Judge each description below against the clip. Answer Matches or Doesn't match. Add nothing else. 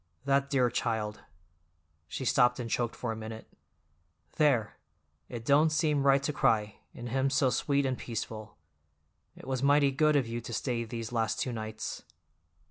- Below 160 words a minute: Doesn't match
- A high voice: Doesn't match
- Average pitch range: Matches